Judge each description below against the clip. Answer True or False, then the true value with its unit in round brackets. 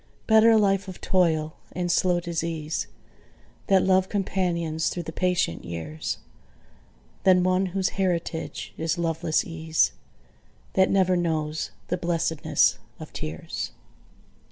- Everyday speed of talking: False (120 wpm)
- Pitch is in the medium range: True (175 Hz)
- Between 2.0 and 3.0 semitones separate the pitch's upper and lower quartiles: True (2.6 semitones)